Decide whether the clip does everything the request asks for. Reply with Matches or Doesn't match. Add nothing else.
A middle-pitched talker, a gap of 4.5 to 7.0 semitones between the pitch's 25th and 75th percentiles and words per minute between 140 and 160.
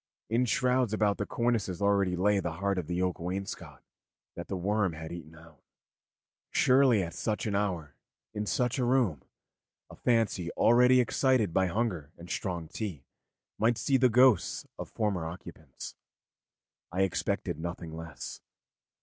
Doesn't match